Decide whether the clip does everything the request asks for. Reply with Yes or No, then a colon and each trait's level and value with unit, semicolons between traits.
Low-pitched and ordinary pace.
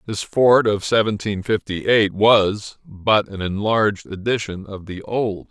Yes: low, 105 Hz; average, 155 wpm